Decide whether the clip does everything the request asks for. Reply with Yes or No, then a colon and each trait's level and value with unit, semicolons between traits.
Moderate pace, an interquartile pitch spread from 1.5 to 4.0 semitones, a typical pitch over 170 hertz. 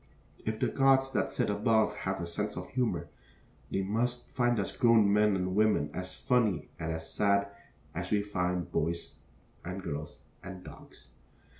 No: average, 170 wpm; average, 3.7 semitones; low, 100 Hz